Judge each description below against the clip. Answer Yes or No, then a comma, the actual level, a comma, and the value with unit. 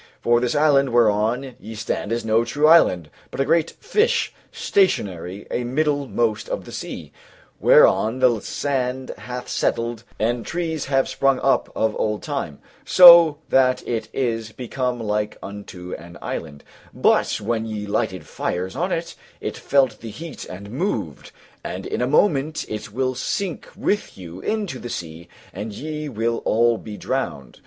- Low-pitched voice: Yes, low, 120 Hz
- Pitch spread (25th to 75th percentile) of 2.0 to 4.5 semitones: No, average, 5.0 semitones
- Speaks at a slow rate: No, average, 160 wpm